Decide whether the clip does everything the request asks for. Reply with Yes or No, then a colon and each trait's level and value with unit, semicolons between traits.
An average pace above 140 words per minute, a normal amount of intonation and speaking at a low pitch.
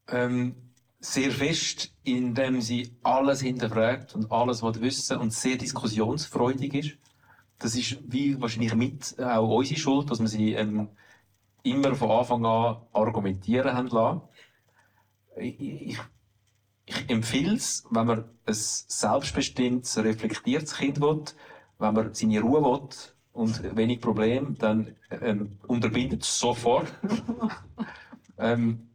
No: slow, 125 wpm; average, 3.1 semitones; low, 120 Hz